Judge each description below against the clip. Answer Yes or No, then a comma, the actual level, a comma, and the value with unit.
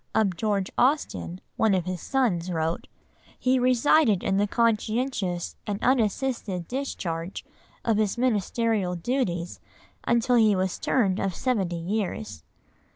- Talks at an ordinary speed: No, slow, 125 wpm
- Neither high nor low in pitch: No, high, 210 Hz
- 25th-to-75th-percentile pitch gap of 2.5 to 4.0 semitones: No, average, 5.0 semitones